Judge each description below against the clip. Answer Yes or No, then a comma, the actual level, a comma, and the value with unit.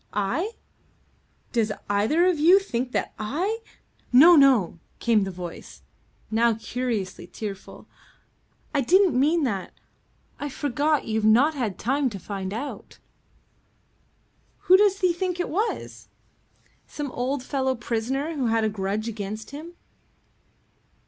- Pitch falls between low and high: No, very high, 255 Hz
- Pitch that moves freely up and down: Yes, wide, 6.4 semitones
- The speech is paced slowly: Yes, slow, 130 wpm